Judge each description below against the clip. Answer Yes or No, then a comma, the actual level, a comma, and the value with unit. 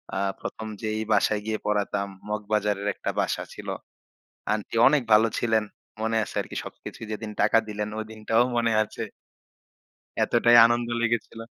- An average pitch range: No, narrow, 1.3 semitones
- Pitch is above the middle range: No, low, 110 Hz